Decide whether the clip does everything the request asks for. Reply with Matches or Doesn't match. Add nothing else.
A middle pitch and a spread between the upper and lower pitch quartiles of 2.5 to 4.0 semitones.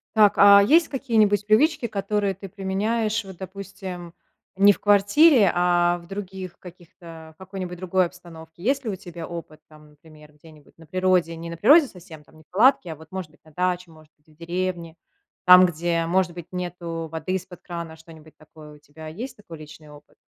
Matches